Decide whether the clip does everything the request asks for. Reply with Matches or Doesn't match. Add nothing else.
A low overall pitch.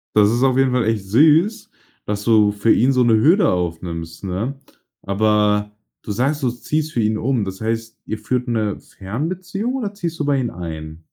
Matches